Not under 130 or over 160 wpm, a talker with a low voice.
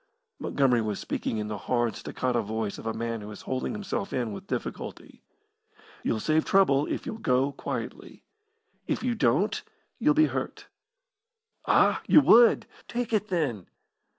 Yes: average, 155 wpm; low, 130 Hz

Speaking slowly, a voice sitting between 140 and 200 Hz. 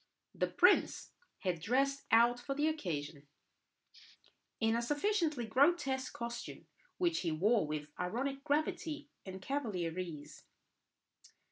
No: slow, 115 wpm; high, 240 Hz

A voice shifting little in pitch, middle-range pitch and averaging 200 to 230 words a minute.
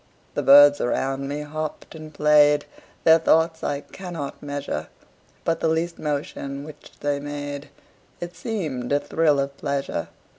No: narrow, 2.3 semitones; medium, 145 Hz; average, 145 wpm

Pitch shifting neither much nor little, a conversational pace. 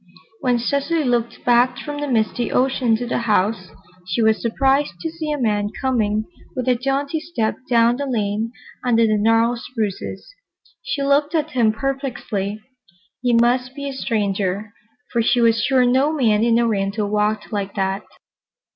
Yes: average, 3.8 semitones; average, 165 wpm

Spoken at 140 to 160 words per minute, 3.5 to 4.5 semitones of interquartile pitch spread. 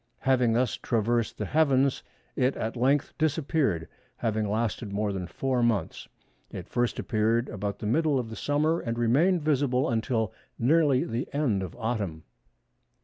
Yes: average, 150 wpm; average, 4.0 semitones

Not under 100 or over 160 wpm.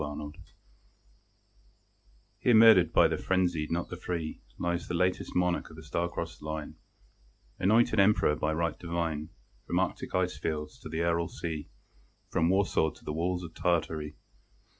Yes: average, 150 wpm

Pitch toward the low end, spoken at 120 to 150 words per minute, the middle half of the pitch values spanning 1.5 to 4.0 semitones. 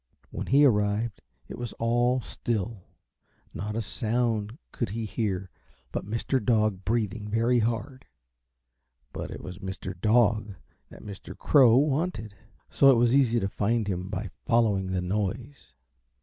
Yes: low, 110 Hz; average, 145 wpm; average, 2.8 semitones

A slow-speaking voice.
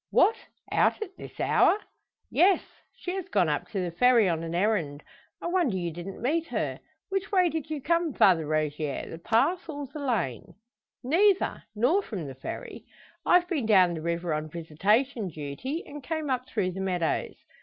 No: average, 180 wpm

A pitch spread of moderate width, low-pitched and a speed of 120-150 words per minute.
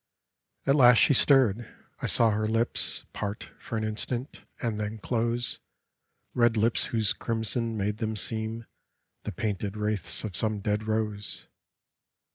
No: narrow, 1.7 semitones; low, 110 Hz; average, 145 wpm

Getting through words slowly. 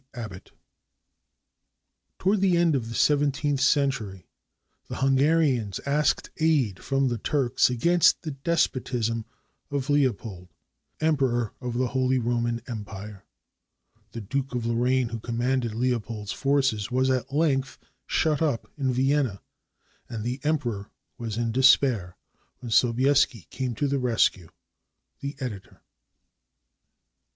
Yes: slow, 125 wpm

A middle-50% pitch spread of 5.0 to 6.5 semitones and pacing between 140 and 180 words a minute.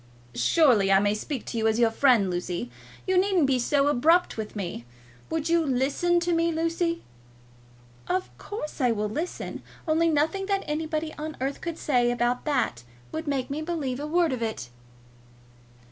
Yes: wide, 5.6 semitones; average, 175 wpm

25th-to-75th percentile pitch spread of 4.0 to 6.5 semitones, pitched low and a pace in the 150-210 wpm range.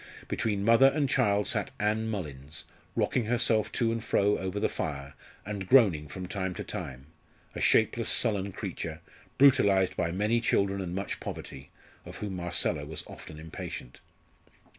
Yes: average, 4.3 semitones; low, 100 Hz; average, 155 wpm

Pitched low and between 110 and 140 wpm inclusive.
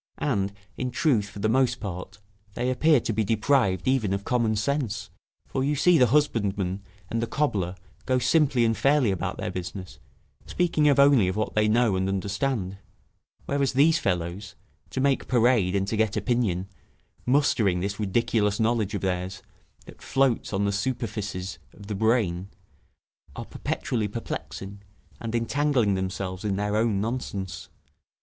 No: low, 110 Hz; average, 155 wpm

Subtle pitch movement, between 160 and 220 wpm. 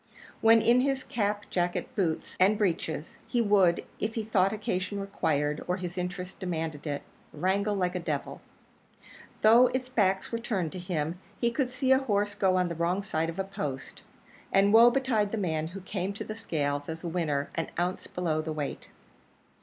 No: average, 4.3 semitones; average, 190 wpm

